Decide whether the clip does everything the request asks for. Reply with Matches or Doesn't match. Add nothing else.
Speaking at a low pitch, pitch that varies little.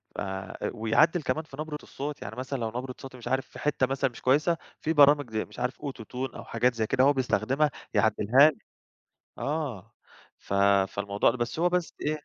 Doesn't match